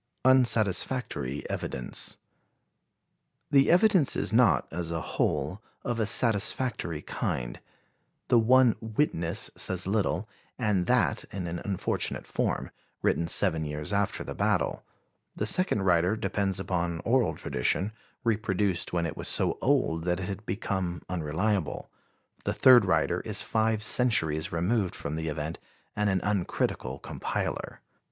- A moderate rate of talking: No, slow, 130 wpm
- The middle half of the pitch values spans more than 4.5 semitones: Yes, average, 5.0 semitones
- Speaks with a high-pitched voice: No, very low, 95 Hz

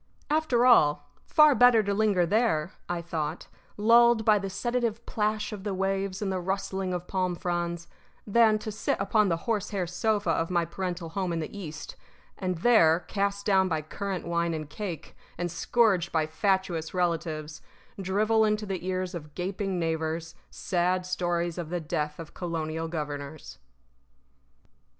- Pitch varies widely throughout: No, average, 3.7 semitones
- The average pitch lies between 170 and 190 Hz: Yes, medium, 185 Hz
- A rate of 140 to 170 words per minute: Yes, average, 160 wpm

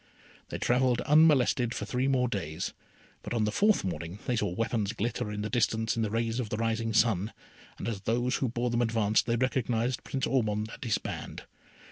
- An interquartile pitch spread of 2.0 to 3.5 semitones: Yes, narrow, 2.5 semitones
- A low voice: Yes, low, 115 Hz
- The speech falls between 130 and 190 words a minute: No, average, 200 wpm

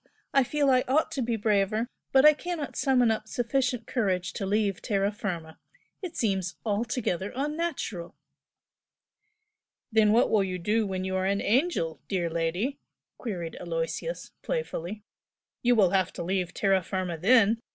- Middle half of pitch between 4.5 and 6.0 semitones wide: Yes, average, 5.2 semitones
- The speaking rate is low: No, average, 150 wpm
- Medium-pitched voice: No, high, 210 Hz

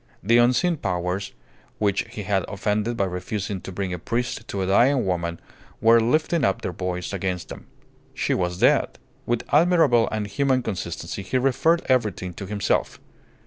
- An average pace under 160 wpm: No, average, 165 wpm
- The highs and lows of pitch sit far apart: No, average, 4.6 semitones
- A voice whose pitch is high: No, low, 105 Hz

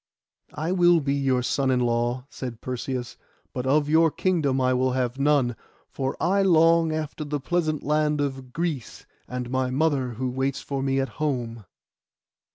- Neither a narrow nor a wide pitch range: Yes, average, 3.3 semitones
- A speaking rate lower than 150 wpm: No, average, 165 wpm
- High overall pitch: No, low, 135 Hz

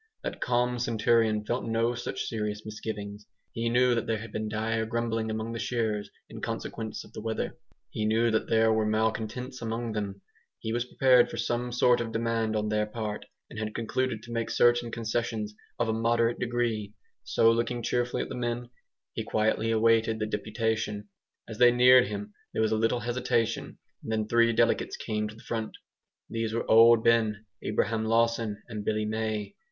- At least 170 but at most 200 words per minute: Yes, average, 185 wpm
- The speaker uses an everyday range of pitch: No, narrow, 1.5 semitones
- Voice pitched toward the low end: Yes, low, 115 Hz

